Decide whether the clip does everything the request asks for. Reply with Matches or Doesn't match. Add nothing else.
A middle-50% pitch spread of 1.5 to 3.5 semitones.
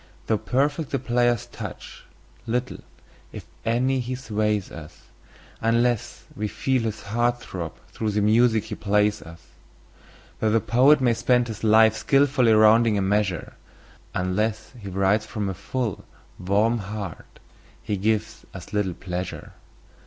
Matches